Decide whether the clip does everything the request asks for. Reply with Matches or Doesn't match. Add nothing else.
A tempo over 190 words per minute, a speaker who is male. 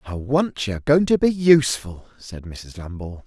Matches